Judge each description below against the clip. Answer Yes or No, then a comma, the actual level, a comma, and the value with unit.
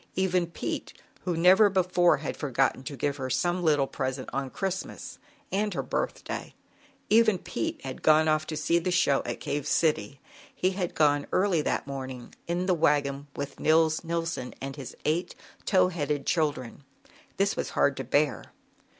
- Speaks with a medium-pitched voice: Yes, medium, 155 Hz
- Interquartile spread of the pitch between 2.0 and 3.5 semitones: No, average, 4.3 semitones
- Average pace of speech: Yes, average, 165 wpm